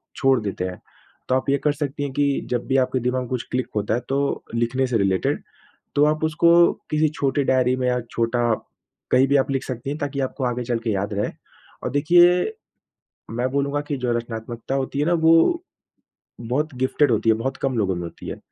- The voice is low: Yes, low, 130 Hz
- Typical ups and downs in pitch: Yes, average, 3.3 semitones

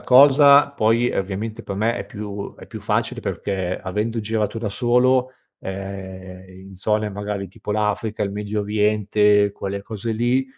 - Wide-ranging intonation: No, narrow, 2.5 semitones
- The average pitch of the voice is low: Yes, low, 105 Hz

